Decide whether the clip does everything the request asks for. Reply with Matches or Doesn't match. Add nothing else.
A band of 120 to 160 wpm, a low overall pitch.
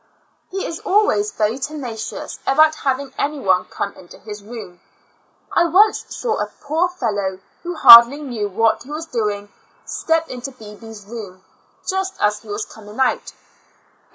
Doesn't match